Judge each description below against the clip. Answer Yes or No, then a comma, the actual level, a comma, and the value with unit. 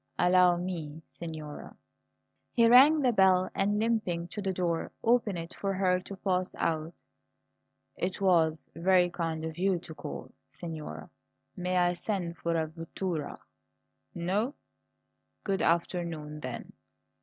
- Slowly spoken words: Yes, slow, 130 wpm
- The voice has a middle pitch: Yes, medium, 180 Hz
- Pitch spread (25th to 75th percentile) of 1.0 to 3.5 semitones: Yes, narrow, 2.6 semitones